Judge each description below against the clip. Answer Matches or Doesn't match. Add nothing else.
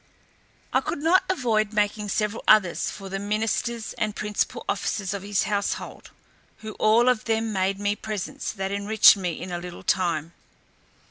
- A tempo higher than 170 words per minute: Doesn't match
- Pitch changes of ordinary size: Doesn't match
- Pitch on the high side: Matches